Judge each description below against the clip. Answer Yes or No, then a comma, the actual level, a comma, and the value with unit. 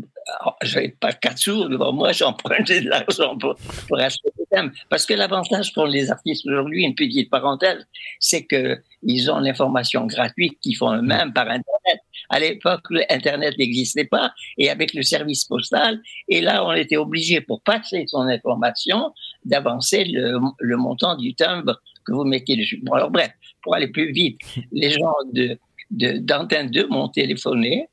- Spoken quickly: No, average, 175 wpm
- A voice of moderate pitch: Yes, medium, 155 Hz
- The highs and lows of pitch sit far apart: Yes, wide, 8.3 semitones